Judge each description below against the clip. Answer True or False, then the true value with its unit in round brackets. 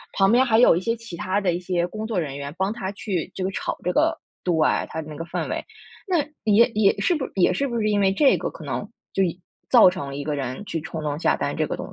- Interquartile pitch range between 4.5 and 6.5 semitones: True (5.0 semitones)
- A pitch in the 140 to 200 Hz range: True (190 Hz)